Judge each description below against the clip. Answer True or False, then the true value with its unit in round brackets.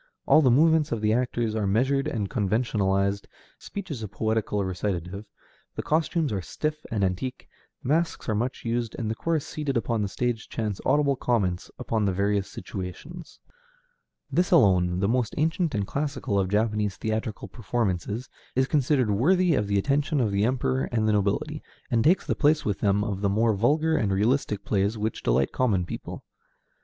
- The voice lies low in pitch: True (110 Hz)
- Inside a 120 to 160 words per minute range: False (175 wpm)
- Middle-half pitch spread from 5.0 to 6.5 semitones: True (5.4 semitones)